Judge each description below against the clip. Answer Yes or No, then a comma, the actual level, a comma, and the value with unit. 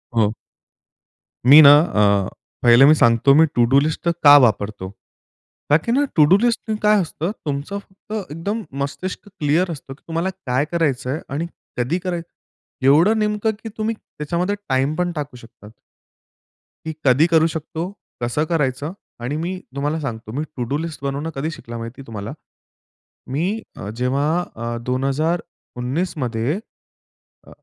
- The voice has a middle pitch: Yes, medium, 150 Hz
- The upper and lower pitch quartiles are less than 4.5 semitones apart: No, average, 4.8 semitones